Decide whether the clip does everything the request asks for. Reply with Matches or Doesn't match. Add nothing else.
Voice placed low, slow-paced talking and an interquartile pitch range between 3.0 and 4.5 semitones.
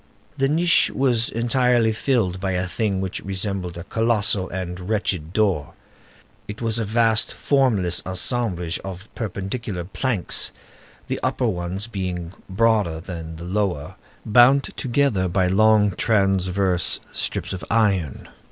Matches